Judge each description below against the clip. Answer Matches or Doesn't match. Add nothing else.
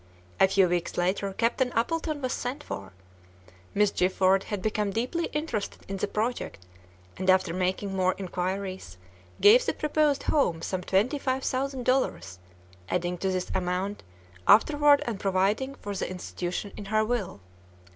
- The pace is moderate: Matches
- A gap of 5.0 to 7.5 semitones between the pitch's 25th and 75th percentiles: Matches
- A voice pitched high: Matches